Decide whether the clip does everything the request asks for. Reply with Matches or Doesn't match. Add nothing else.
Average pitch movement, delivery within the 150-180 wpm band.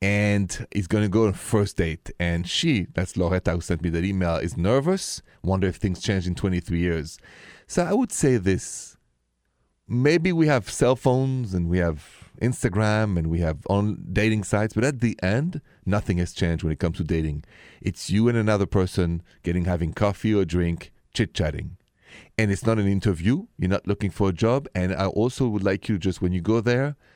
Doesn't match